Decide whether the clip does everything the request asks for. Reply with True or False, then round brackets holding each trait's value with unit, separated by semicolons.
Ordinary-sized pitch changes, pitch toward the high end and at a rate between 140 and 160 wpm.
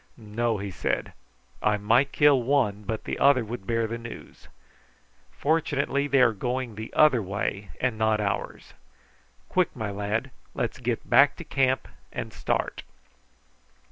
False (4.1 semitones; 115 Hz; 145 wpm)